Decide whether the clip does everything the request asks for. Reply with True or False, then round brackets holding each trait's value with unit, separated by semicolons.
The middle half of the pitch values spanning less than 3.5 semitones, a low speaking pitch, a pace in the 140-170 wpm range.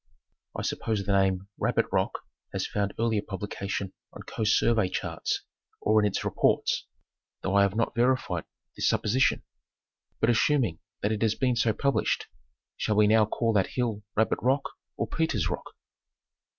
True (2.7 semitones; 110 Hz; 160 wpm)